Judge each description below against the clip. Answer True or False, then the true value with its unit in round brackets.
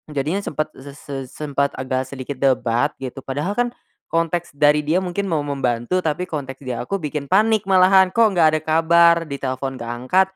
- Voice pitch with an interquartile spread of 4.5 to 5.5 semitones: True (5.1 semitones)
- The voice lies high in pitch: False (150 Hz)